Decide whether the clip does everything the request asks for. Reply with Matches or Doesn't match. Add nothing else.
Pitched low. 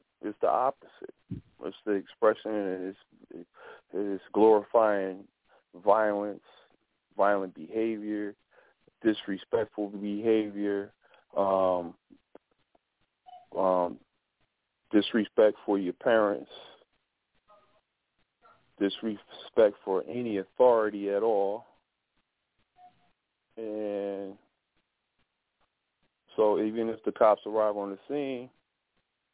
Matches